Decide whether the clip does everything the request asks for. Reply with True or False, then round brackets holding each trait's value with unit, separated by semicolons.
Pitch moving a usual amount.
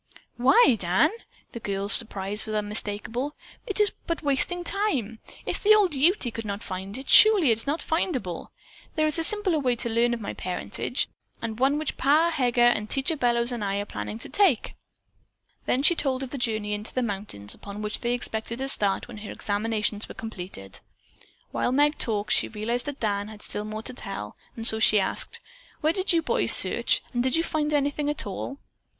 False (5.9 semitones)